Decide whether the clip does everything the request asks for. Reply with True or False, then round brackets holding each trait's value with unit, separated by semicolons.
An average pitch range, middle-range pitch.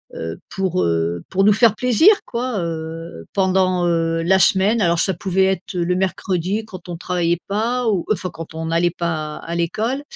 True (3.2 semitones; 180 Hz)